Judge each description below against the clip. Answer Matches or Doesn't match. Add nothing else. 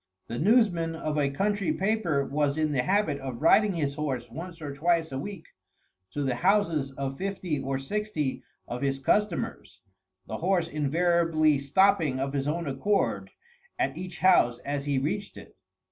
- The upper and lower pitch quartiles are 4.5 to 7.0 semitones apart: Matches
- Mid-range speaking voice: Matches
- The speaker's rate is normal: Matches